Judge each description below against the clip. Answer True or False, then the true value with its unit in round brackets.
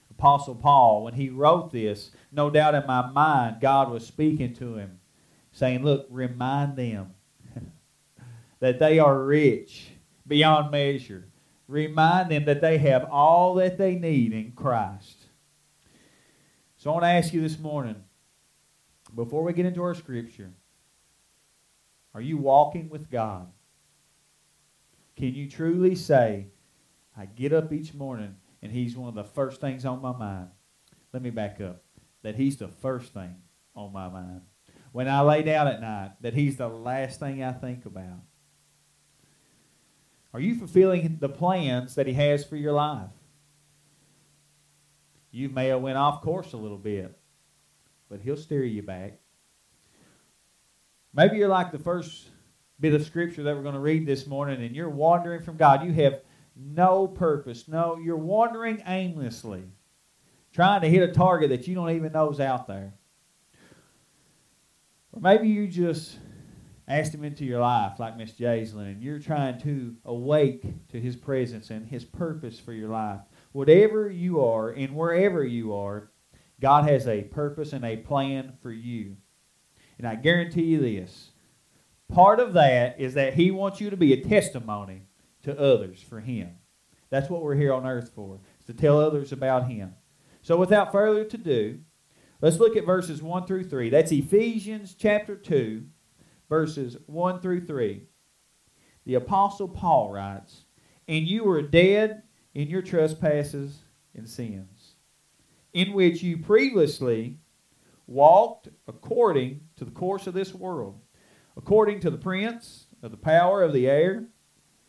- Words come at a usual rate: True (155 wpm)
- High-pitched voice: False (140 Hz)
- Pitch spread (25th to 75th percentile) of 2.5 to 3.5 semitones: False (5.6 semitones)